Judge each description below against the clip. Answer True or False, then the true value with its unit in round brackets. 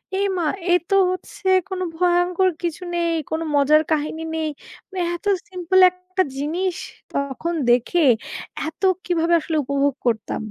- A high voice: True (340 Hz)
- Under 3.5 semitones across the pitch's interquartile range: True (3.1 semitones)